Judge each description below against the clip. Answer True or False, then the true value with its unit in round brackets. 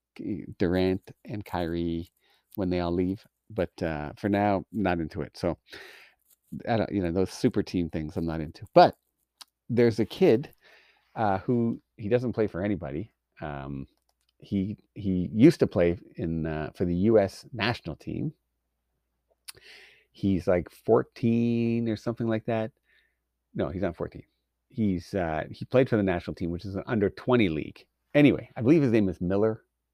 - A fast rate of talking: False (165 wpm)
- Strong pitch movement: False (4.9 semitones)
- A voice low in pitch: True (95 Hz)